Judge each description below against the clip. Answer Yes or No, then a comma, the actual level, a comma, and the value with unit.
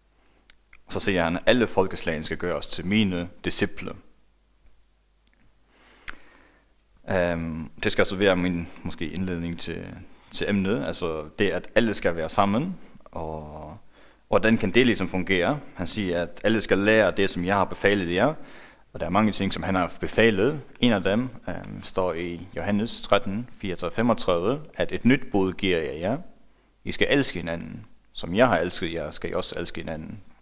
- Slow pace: No, average, 175 wpm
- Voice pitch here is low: Yes, very low, 90 Hz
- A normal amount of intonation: Yes, average, 3.2 semitones